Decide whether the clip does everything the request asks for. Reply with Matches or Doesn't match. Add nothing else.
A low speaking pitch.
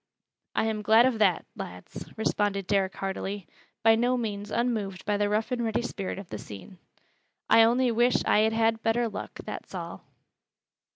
Doesn't match